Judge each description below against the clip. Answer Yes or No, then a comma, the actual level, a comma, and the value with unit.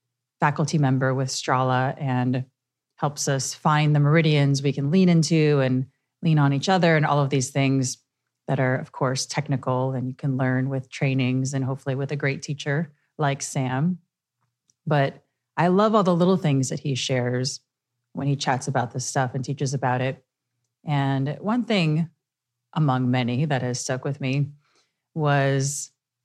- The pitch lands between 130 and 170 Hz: Yes, low, 135 Hz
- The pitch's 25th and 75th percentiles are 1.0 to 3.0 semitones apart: Yes, narrow, 2.4 semitones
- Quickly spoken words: No, average, 170 wpm